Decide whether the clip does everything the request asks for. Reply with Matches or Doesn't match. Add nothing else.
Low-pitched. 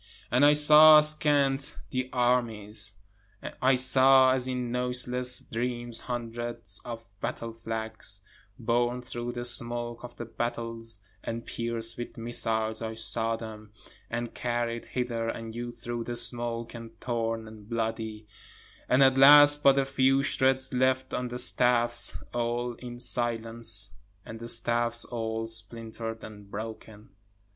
Matches